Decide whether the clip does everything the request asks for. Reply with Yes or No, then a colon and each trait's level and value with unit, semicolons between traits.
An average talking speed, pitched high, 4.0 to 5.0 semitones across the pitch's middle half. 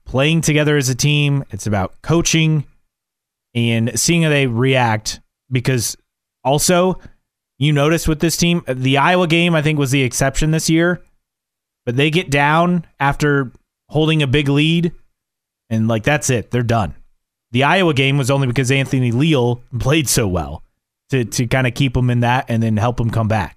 No: average, 180 wpm; low, 135 Hz; average, 4.6 semitones